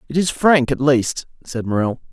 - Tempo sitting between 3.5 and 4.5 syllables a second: No, 4.7 syllables/s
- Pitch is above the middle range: No, low, 135 Hz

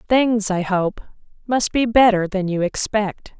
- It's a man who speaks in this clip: No, female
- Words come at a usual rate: Yes, average, 160 wpm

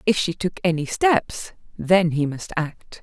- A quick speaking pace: No, average, 180 wpm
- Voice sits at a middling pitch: Yes, medium, 175 Hz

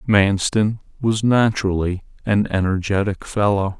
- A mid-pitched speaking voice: No, low, 100 Hz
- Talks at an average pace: No, slow, 95 wpm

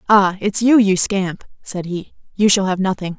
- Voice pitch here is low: No, high, 195 Hz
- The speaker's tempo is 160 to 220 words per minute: Yes, fast, 205 wpm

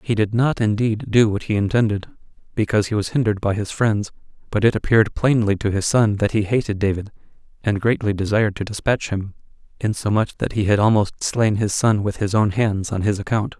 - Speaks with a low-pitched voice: Yes, low, 105 Hz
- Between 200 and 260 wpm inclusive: Yes, fast, 205 wpm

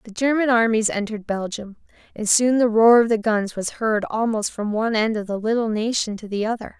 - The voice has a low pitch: No, high, 220 Hz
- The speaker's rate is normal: No, fast, 220 wpm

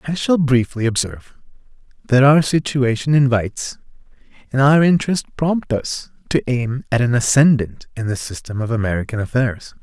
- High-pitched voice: No, low, 125 Hz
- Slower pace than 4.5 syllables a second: No, 5.1 syllables/s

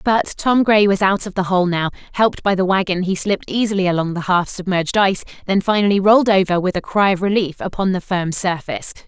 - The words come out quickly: Yes, fast, 225 wpm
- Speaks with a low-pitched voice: No, high, 190 Hz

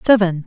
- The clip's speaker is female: Yes, female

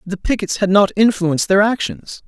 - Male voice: Yes, male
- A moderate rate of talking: Yes, average, 185 wpm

